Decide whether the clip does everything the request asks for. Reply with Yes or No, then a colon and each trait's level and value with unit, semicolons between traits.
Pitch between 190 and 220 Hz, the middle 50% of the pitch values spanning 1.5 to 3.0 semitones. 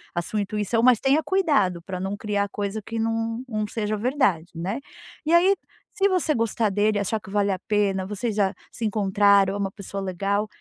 Yes: high, 210 Hz; narrow, 2.6 semitones